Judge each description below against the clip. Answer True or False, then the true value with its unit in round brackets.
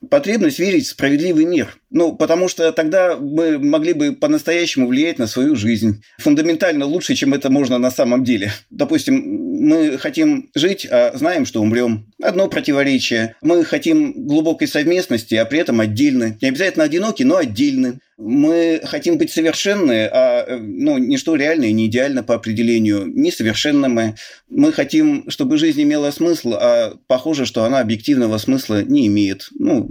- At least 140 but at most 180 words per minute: True (155 wpm)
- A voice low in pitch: False (255 Hz)